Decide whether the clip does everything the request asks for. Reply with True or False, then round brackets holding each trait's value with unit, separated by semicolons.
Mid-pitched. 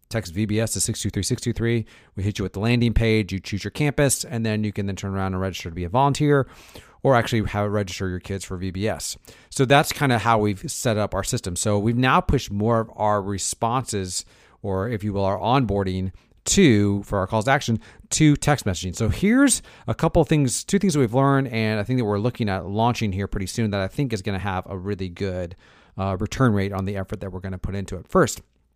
False (105 Hz)